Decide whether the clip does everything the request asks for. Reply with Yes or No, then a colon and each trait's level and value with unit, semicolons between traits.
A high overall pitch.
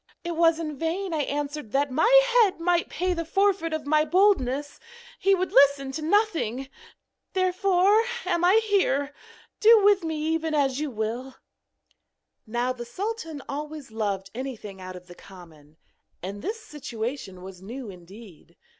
Yes: very high, 295 Hz